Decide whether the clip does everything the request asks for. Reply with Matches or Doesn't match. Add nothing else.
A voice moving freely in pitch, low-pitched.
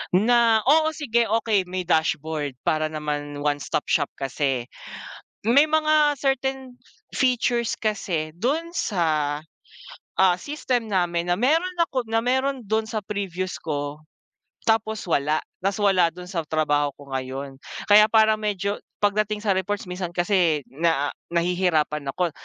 Doesn't match